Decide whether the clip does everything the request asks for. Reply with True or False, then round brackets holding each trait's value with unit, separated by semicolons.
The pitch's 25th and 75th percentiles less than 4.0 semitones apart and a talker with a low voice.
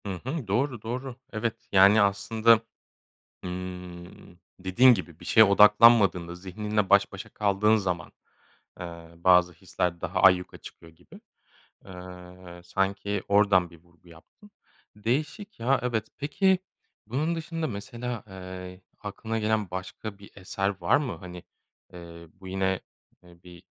True (3.6 semitones; 95 Hz)